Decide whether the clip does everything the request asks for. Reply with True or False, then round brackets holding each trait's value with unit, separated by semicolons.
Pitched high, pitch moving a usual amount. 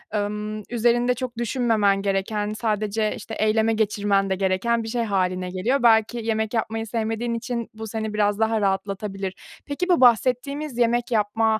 False (220 Hz; 2.3 semitones)